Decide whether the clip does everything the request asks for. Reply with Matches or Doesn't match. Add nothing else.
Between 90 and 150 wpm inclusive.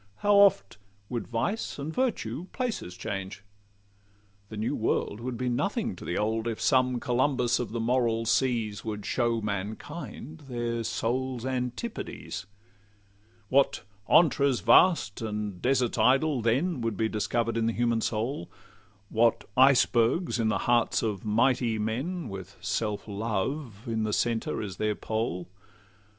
Matches